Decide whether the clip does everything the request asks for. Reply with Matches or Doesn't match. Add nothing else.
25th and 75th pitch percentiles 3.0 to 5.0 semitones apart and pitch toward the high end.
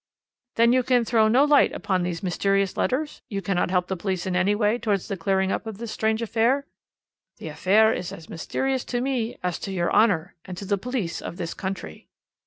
Matches